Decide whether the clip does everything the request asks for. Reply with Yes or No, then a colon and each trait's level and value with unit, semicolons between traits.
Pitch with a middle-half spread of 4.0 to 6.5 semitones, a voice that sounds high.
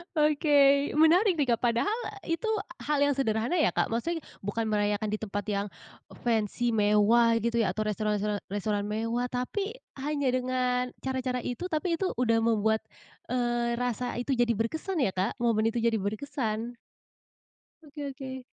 Yes: average, 4.4 semitones; high, 240 Hz